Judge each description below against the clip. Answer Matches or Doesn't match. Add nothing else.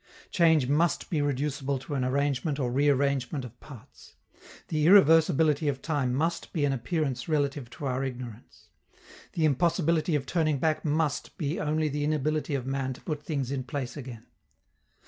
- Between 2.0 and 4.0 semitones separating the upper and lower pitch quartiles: Matches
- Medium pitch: Matches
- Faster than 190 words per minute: Doesn't match